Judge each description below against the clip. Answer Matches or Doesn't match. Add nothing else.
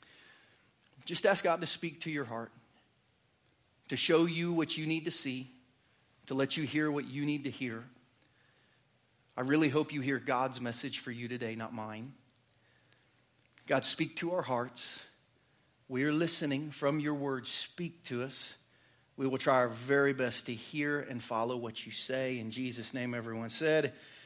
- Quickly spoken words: Doesn't match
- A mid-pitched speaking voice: Doesn't match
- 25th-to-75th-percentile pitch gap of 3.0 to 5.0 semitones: Matches